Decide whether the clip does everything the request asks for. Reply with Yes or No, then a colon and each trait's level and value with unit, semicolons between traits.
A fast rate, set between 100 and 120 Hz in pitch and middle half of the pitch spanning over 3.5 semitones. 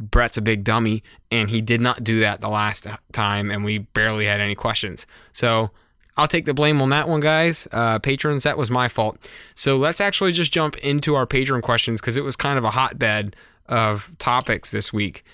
Yes: fast, 210 wpm; low, 115 Hz; average, 4.6 semitones